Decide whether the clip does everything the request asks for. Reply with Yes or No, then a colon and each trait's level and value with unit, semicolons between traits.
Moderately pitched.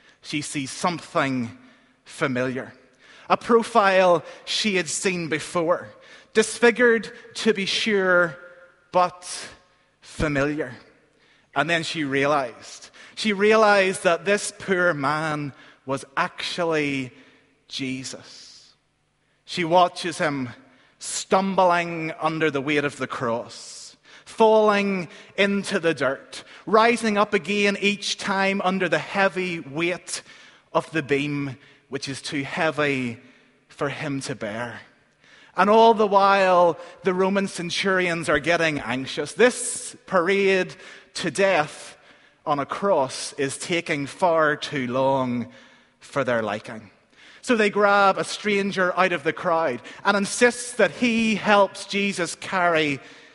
Yes: medium, 175 Hz